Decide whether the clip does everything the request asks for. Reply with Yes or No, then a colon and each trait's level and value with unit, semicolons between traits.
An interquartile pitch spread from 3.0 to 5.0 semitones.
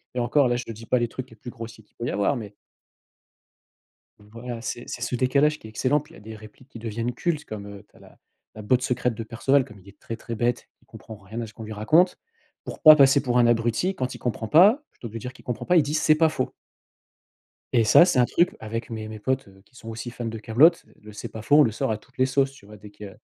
Yes: average, 3.3 semitones